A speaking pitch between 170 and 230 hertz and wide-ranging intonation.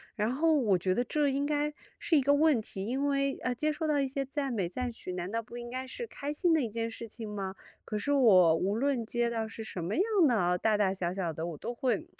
No: high, 240 Hz; wide, 5.7 semitones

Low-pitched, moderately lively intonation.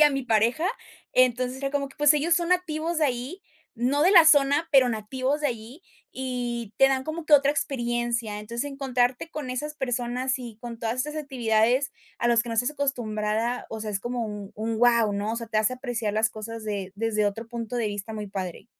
No: high, 245 Hz; average, 3.7 semitones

